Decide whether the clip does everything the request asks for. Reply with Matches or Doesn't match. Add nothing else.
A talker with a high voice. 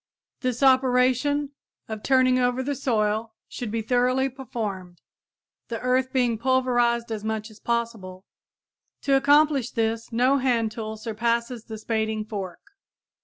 Matches